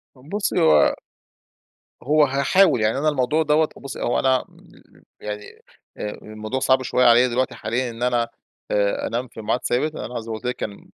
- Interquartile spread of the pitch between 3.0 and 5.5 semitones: Yes, average, 3.4 semitones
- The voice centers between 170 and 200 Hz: No, low, 125 Hz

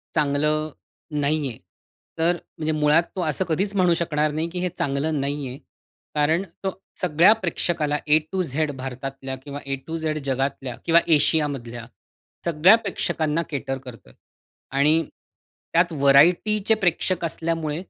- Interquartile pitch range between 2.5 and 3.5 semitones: Yes, average, 3.2 semitones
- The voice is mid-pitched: Yes, medium, 155 Hz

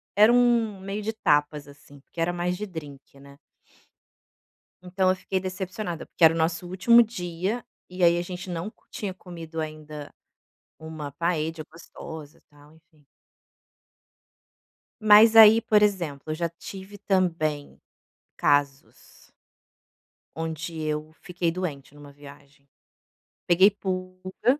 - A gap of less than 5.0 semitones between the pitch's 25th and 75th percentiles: Yes, average, 3.8 semitones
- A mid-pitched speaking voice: Yes, medium, 170 Hz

